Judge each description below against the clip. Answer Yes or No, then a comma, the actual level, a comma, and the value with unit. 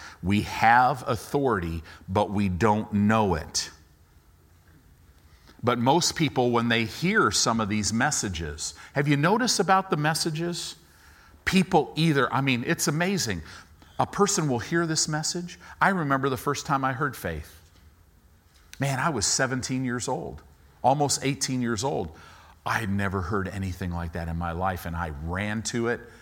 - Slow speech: No, average, 160 wpm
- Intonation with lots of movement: Yes, wide, 8.9 semitones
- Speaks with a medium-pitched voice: No, low, 110 Hz